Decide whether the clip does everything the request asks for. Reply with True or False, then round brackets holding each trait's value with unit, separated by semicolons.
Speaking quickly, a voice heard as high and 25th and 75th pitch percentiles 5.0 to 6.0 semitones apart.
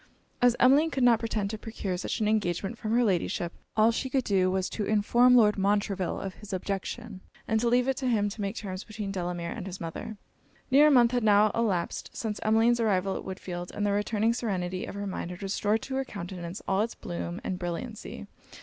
False (215 wpm; 210 Hz; 3.6 semitones)